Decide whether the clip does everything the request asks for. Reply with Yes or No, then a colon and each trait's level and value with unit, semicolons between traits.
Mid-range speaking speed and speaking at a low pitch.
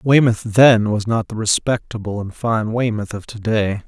Yes: average, 185 wpm; low, 110 Hz